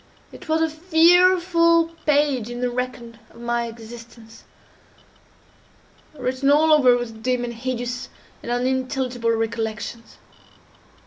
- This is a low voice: No, very high, 250 Hz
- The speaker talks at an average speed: No, slow, 110 wpm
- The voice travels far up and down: No, average, 4.3 semitones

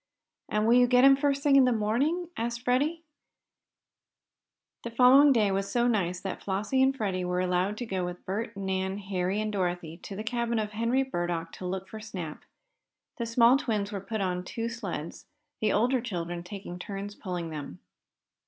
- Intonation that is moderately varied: Yes, average, 4.6 semitones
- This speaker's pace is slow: No, average, 185 wpm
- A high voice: Yes, high, 210 Hz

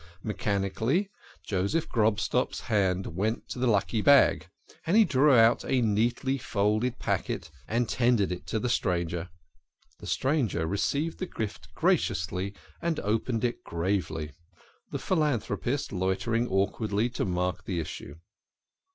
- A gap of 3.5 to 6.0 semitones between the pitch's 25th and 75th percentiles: Yes, average, 4.8 semitones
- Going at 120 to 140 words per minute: Yes, slow, 135 wpm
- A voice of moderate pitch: No, low, 110 Hz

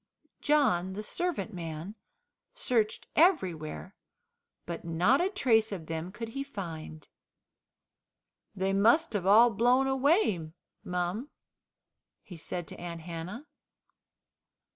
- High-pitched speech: Yes, high, 200 Hz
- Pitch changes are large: Yes, wide, 6.8 semitones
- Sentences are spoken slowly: Yes, slow, 110 wpm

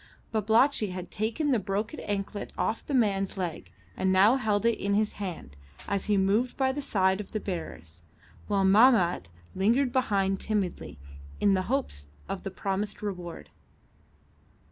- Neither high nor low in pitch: No, high, 200 Hz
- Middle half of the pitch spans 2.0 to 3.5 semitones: Yes, average, 2.8 semitones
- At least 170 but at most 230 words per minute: No, average, 155 wpm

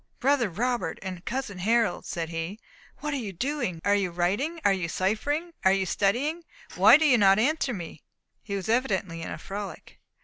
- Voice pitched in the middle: No, high, 205 Hz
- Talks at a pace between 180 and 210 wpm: Yes, average, 190 wpm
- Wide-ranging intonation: Yes, wide, 6.1 semitones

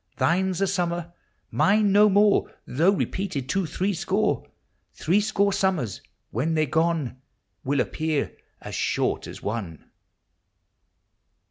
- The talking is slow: Yes, slow, 115 wpm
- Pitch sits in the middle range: Yes, medium, 175 Hz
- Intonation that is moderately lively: Yes, average, 4.7 semitones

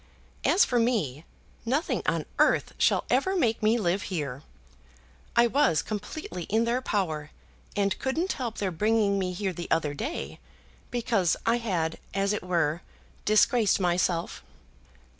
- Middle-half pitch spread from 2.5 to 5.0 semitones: No, wide, 5.4 semitones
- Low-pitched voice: No, high, 205 Hz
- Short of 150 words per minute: Yes, average, 140 wpm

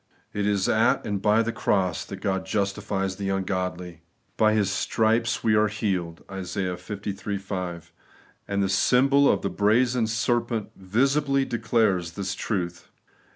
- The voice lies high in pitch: No, low, 100 Hz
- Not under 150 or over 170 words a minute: Yes, average, 155 wpm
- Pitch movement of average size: Yes, average, 3.0 semitones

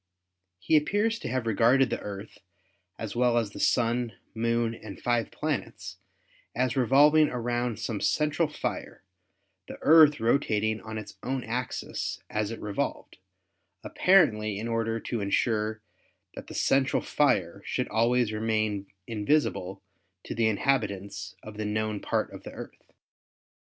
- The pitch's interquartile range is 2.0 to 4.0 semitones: Yes, average, 3.0 semitones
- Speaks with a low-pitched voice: Yes, low, 115 Hz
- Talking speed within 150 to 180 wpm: No, average, 140 wpm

